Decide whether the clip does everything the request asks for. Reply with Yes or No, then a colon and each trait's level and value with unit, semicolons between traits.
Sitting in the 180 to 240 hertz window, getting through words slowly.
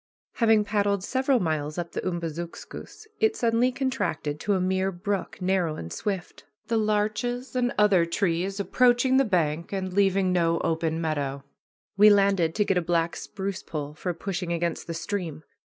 No: high, 190 Hz; average, 165 wpm